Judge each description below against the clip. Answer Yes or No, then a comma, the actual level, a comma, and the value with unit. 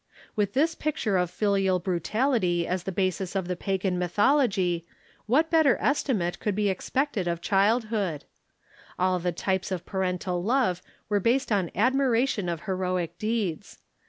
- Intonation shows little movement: No, average, 4.3 semitones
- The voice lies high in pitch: Yes, high, 195 Hz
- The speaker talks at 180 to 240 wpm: No, average, 145 wpm